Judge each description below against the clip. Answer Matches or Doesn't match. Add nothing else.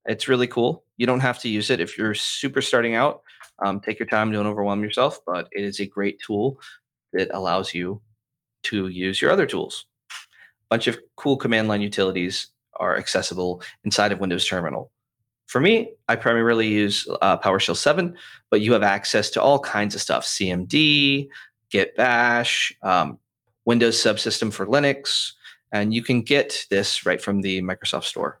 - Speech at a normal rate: Matches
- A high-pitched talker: Doesn't match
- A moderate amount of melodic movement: Matches